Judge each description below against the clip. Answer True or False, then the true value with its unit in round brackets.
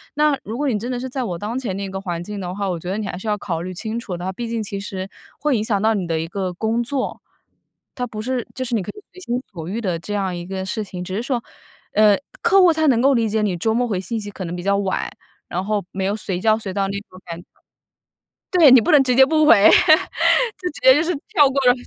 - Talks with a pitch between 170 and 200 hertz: False (210 Hz)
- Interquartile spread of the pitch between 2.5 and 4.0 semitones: False (4.7 semitones)